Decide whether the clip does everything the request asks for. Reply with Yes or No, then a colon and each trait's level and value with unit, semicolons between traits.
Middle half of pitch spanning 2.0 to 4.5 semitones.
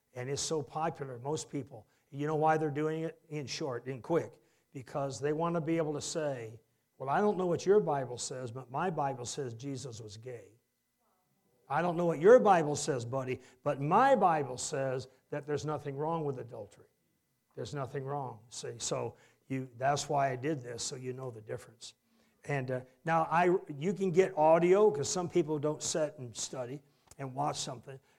Yes: average, 3.5 semitones